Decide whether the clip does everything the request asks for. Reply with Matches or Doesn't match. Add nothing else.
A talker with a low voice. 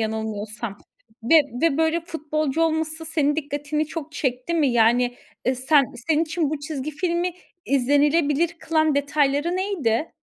Doesn't match